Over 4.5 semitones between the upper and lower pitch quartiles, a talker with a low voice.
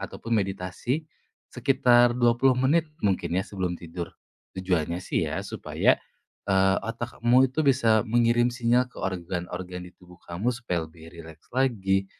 Yes: average, 5.3 semitones; low, 100 Hz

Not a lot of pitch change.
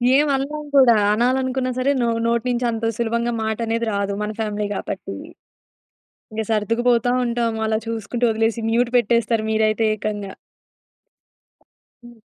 Yes: narrow, 1.8 semitones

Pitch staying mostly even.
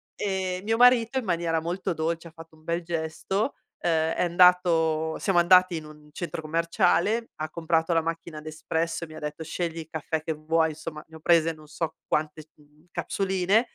Yes: narrow, 2.0 semitones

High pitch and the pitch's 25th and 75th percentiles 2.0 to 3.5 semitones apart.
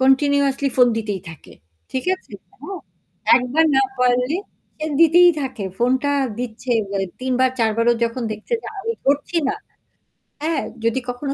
Yes: very high, 260 Hz; average, 3.2 semitones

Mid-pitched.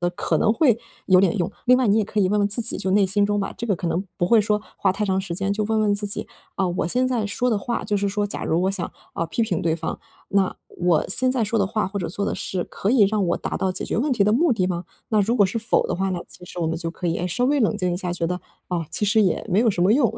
No: high, 200 Hz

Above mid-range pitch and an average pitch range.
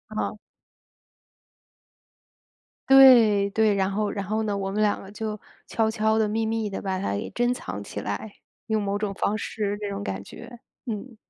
No: high, 210 Hz; narrow, 1.8 semitones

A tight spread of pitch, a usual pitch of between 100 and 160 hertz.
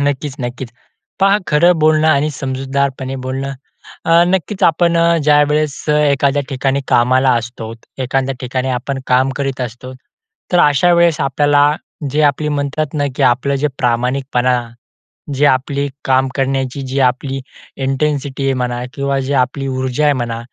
Yes: narrow, 2.1 semitones; low, 135 Hz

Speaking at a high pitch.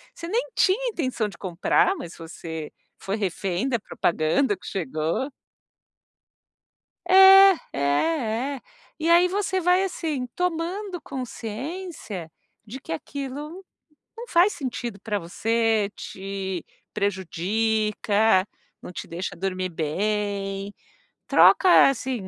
Yes: high, 220 Hz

